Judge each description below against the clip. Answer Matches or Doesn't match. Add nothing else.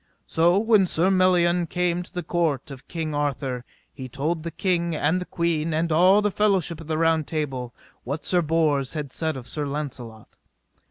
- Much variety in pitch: Doesn't match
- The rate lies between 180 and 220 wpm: Matches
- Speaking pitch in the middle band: Matches